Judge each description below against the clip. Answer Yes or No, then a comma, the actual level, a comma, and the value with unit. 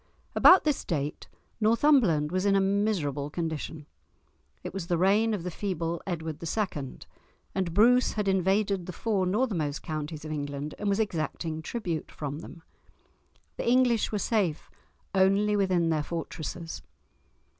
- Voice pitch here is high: No, medium, 180 Hz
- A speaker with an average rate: Yes, average, 145 wpm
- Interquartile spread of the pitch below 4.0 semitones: No, average, 4.7 semitones